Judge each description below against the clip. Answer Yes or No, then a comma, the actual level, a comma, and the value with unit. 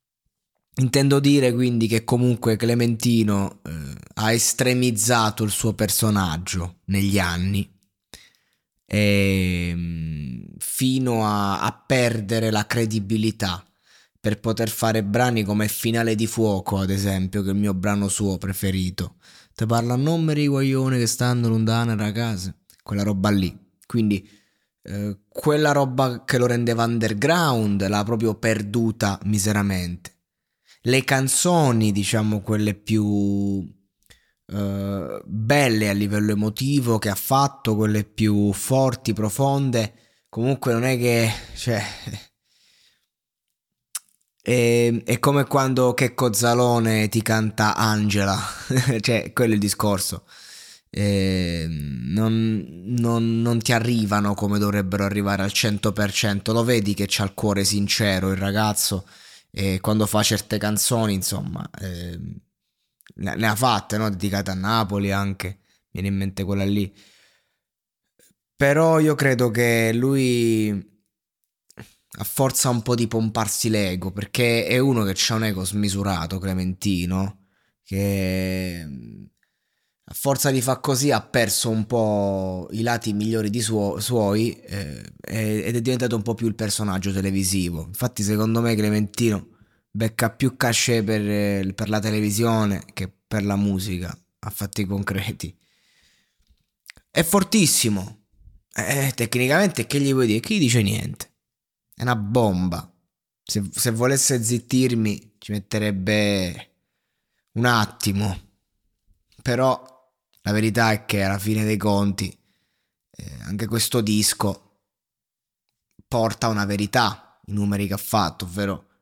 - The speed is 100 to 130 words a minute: Yes, average, 125 wpm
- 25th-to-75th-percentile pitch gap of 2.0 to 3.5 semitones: Yes, average, 2.9 semitones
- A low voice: Yes, low, 105 Hz